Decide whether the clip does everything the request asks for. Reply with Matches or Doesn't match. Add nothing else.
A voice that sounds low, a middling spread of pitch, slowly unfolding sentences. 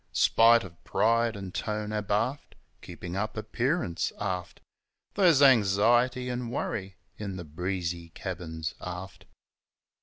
Matches